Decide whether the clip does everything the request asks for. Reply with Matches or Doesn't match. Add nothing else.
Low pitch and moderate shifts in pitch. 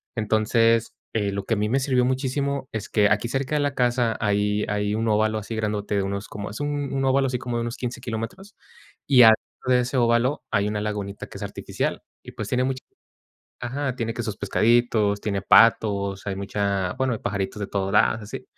Matches